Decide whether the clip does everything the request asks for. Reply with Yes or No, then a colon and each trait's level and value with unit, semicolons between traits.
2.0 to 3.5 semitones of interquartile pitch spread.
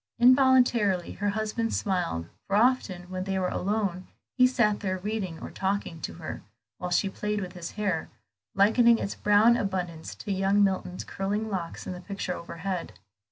Yes: average, 2.8 semitones